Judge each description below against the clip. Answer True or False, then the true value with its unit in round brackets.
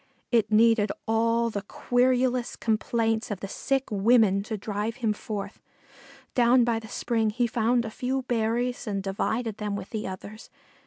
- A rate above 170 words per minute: False (160 wpm)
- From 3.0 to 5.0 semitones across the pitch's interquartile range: False (2.4 semitones)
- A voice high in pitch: True (225 Hz)